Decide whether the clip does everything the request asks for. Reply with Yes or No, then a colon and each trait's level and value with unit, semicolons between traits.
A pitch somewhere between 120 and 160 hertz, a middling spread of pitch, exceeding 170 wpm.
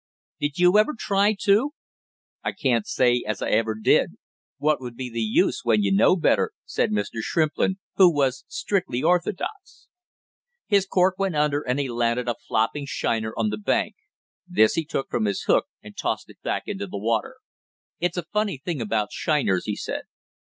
No: medium, 140 Hz; wide, 8.1 semitones; average, 180 wpm